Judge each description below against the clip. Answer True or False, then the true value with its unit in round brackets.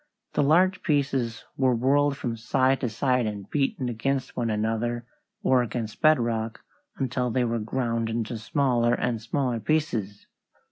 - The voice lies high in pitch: False (120 Hz)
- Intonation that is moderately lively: True (3.1 semitones)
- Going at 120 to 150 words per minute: True (145 wpm)